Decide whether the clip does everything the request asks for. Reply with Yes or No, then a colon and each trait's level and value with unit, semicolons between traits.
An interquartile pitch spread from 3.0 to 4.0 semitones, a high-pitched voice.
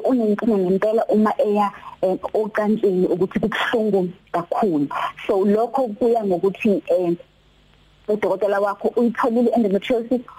Yes: average, 3.4 semitones; high, 210 Hz